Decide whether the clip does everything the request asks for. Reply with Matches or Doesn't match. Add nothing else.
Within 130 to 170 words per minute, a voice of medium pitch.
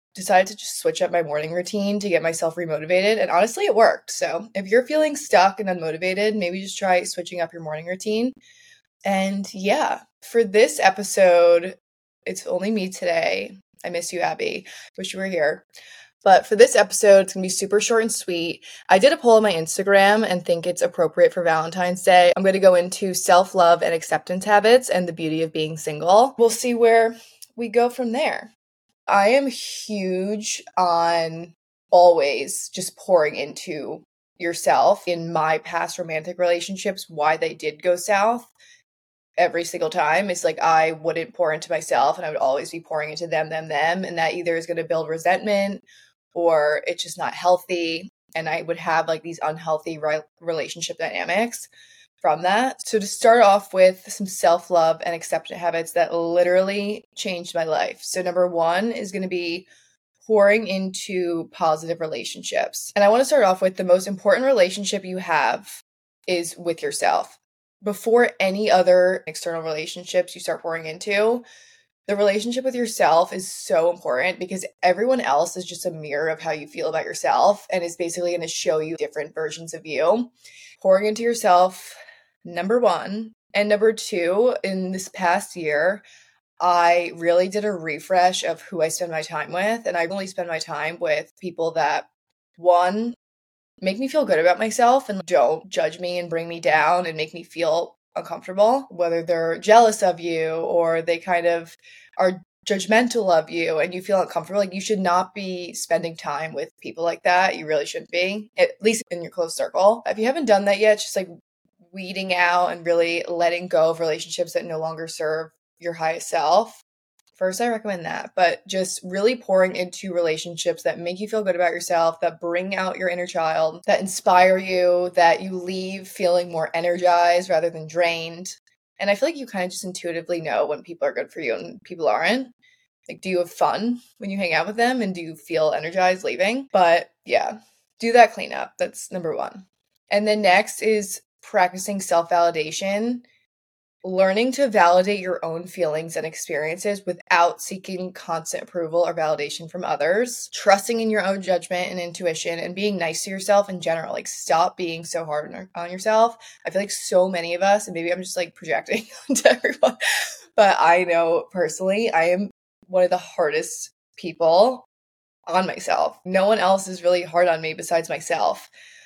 Doesn't match